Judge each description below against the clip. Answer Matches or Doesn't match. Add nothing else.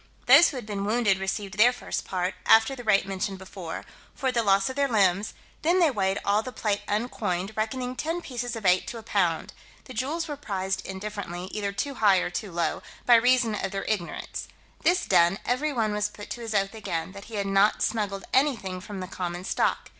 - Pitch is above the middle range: Matches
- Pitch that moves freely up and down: Doesn't match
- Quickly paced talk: Matches